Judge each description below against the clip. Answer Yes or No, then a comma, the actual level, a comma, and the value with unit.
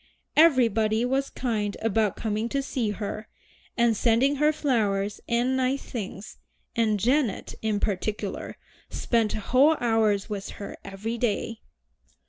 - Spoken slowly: Yes, slow, 125 wpm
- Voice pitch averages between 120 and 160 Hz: No, high, 225 Hz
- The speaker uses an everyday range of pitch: Yes, average, 3.4 semitones